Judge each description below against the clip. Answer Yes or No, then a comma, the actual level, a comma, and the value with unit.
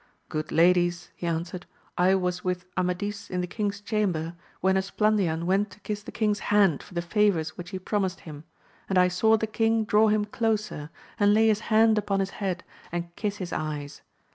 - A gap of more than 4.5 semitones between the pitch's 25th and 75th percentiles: No, average, 3.1 semitones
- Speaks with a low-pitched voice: No, high, 190 Hz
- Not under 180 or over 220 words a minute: Yes, average, 190 wpm